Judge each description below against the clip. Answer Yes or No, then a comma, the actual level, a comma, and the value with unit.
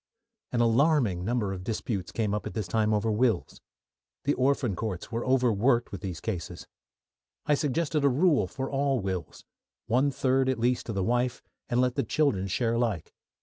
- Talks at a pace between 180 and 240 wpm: Yes, average, 185 wpm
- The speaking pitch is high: No, low, 120 Hz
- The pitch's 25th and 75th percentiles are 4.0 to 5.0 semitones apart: Yes, average, 4.3 semitones